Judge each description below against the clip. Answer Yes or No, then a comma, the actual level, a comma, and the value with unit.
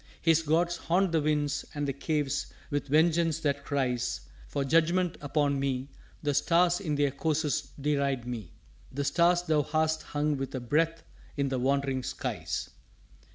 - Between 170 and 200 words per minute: No, average, 155 wpm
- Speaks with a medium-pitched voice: Yes, medium, 145 Hz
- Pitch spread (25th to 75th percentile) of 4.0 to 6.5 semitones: No, average, 2.8 semitones